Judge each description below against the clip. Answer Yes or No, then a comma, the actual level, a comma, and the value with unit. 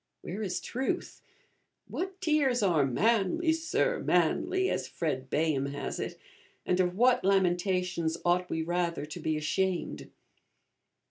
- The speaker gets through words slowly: Yes, slow, 130 wpm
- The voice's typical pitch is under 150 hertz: No, medium, 180 Hz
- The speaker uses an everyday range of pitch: No, wide, 7.0 semitones